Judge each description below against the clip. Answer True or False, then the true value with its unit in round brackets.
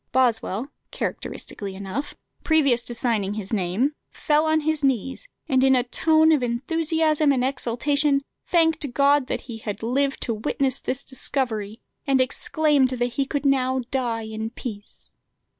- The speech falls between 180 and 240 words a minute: False (150 wpm)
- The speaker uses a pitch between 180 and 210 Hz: False (260 Hz)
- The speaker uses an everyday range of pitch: True (3.8 semitones)